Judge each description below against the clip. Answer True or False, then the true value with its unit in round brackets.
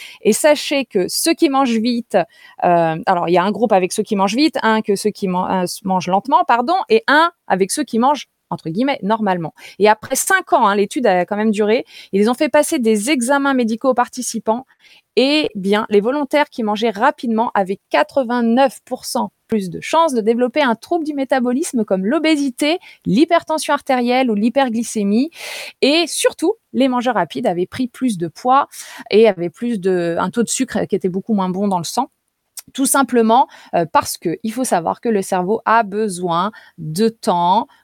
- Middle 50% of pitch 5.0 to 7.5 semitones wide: True (5.3 semitones)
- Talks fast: False (185 wpm)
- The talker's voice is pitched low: False (235 Hz)